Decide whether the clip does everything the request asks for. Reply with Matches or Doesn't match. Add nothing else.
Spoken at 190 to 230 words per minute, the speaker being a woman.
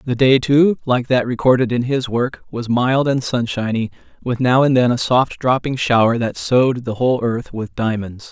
Doesn't match